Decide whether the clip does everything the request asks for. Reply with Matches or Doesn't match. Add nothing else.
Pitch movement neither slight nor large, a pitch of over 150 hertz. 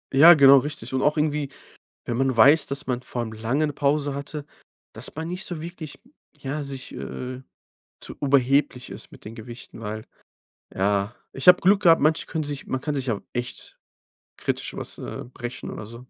Doesn't match